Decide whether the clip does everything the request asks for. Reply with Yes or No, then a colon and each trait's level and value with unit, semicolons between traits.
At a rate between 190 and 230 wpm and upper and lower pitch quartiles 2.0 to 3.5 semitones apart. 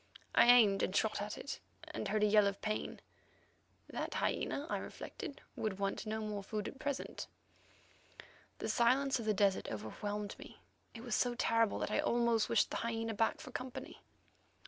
No: average, 175 wpm; narrow, 2.5 semitones